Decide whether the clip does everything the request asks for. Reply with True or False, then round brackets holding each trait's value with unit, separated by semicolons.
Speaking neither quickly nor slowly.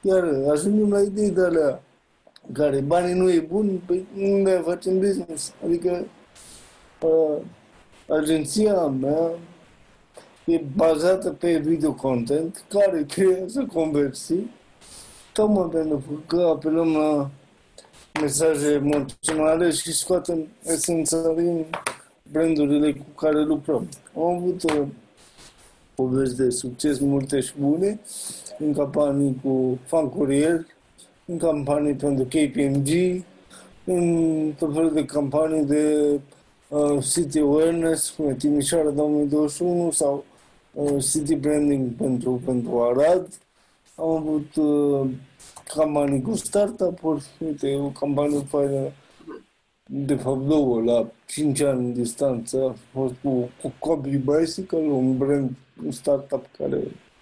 False (115 wpm)